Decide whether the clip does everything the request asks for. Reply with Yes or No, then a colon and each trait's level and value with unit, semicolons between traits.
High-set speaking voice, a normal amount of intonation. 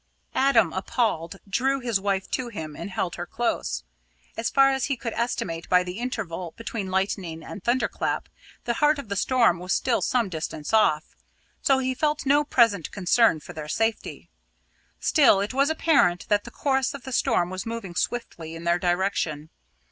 No: high, 210 Hz; wide, 6.2 semitones